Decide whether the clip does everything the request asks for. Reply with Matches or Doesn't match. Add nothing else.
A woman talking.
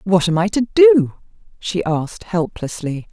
Matches